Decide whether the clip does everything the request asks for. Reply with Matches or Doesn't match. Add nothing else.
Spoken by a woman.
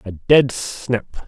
Doesn't match